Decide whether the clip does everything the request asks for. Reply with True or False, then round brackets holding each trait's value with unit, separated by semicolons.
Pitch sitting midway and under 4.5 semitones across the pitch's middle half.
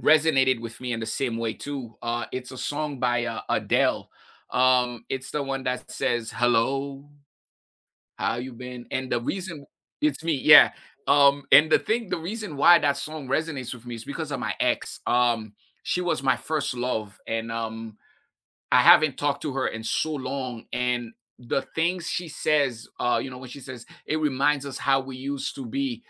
False (130 Hz; 3.5 semitones)